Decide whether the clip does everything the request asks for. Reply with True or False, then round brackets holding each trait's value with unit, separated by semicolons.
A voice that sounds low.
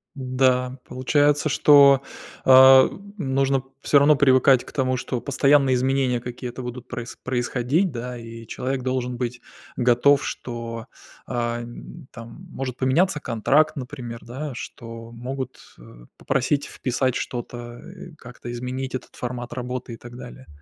True (130 Hz)